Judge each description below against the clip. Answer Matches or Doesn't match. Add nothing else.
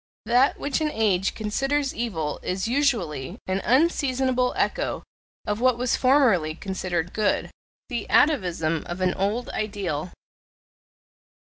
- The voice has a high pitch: Matches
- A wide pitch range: Matches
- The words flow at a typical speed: Doesn't match